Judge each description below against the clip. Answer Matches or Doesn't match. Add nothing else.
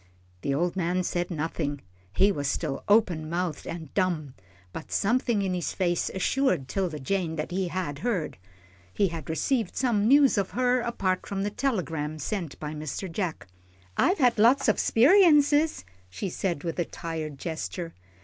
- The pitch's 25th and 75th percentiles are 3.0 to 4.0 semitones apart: Doesn't match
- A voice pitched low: Doesn't match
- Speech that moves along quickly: Doesn't match